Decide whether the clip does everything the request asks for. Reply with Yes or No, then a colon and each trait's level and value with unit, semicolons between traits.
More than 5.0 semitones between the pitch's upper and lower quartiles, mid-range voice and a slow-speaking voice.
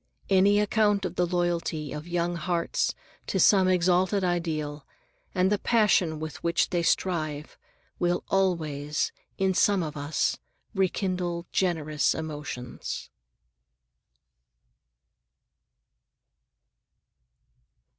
No: average, 3.3 semitones; medium, 175 Hz; slow, 95 wpm